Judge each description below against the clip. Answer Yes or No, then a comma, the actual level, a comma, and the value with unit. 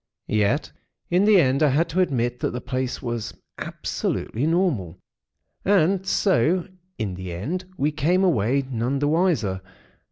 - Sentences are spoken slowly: No, average, 155 wpm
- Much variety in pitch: Yes, wide, 7.0 semitones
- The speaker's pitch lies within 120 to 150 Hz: Yes, medium, 140 Hz